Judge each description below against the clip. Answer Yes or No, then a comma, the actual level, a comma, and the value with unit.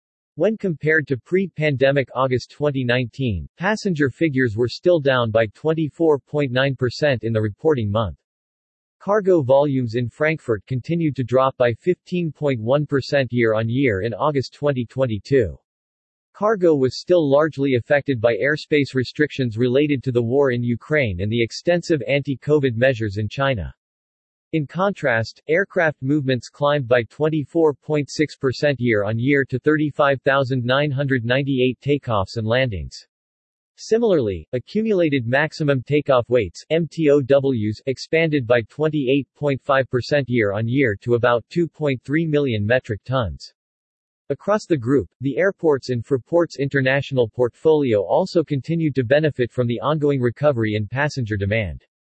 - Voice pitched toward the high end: No, low, 135 Hz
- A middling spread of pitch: Yes, average, 3.7 semitones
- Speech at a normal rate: No, slow, 120 wpm